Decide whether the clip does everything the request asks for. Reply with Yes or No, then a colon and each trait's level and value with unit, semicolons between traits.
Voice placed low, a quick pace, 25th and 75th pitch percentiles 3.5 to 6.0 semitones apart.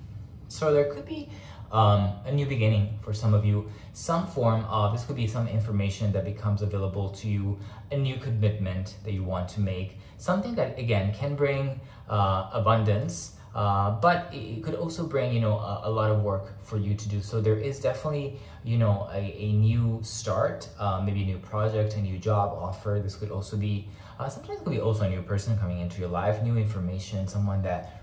No: low, 105 Hz; fast, 210 wpm; narrow, 2.4 semitones